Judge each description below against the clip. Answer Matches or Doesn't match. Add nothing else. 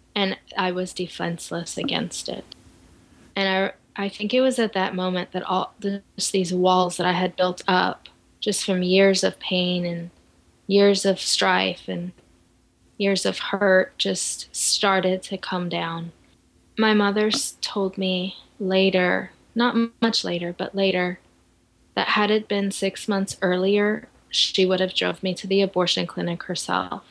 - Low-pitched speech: Doesn't match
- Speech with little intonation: Matches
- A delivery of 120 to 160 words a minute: Matches